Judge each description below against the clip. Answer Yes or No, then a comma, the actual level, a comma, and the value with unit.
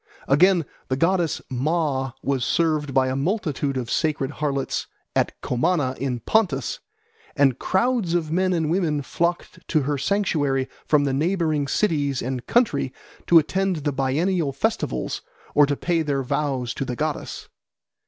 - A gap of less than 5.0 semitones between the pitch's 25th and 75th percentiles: Yes, average, 4.2 semitones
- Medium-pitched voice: Yes, medium, 150 Hz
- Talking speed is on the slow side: No, average, 150 wpm